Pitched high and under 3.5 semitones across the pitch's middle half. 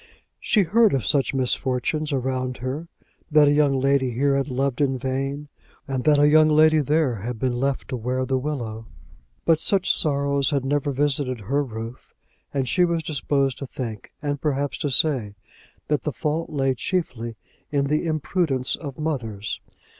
No: medium, 140 Hz; average, 2.8 semitones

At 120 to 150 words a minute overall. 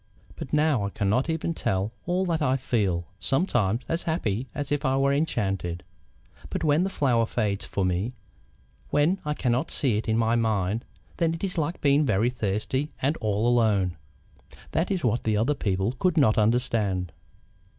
No: average, 175 wpm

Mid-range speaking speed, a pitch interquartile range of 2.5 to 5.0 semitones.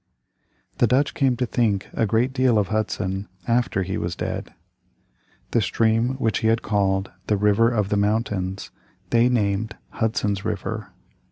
Yes: average, 155 wpm; average, 2.9 semitones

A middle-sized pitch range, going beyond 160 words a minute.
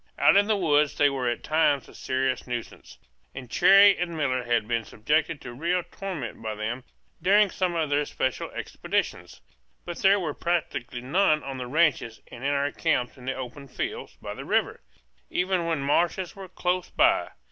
No: wide, 5.8 semitones; average, 185 wpm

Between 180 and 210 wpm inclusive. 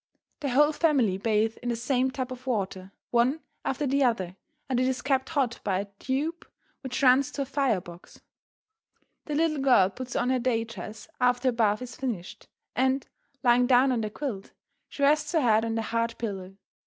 Yes: average, 195 wpm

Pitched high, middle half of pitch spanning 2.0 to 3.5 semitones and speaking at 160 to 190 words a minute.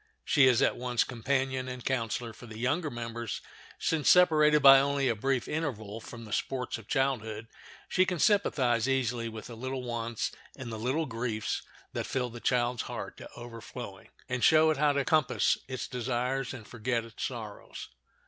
No: low, 125 Hz; average, 2.8 semitones; average, 175 wpm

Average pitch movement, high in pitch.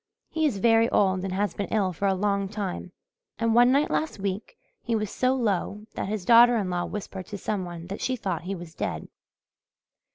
Yes: average, 3.4 semitones; high, 205 Hz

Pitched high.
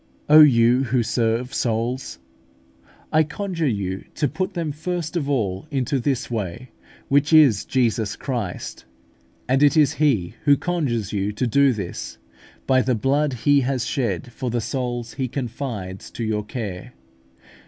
No: low, 125 Hz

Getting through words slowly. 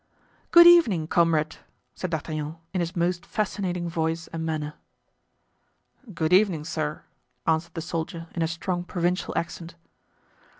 Yes: slow, 130 wpm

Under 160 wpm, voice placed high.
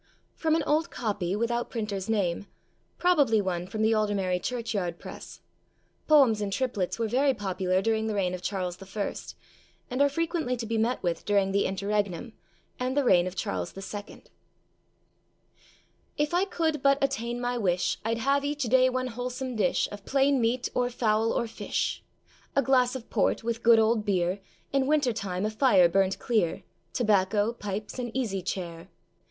No: average, 170 wpm; high, 225 Hz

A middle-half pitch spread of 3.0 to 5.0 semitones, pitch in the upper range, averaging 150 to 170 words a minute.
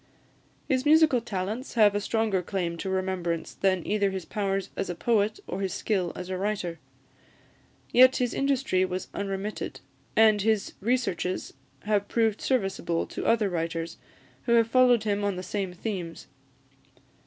Yes: average, 3.3 semitones; high, 200 Hz; average, 155 wpm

